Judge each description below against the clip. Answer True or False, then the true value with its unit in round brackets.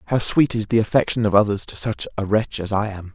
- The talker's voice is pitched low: True (105 Hz)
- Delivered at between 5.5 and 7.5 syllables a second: True (6.0 syllables/s)